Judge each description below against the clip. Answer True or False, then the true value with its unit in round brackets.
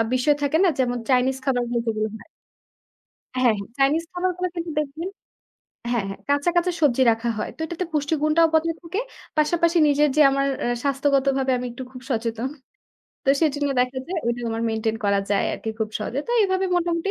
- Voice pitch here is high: True (275 Hz)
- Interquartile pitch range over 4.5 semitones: True (5.2 semitones)